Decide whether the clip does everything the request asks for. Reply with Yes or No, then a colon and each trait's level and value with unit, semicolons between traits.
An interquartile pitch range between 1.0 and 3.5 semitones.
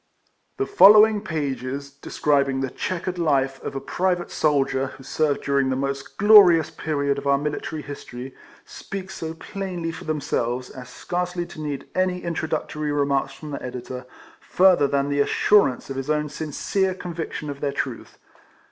No: average, 4.2 semitones